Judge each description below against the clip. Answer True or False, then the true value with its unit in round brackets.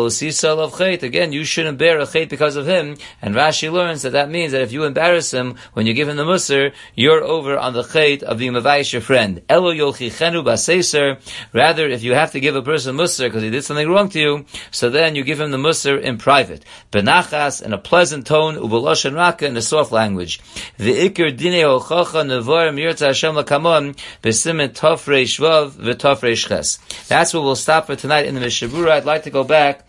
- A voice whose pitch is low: False (145 Hz)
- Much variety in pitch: False (3.5 semitones)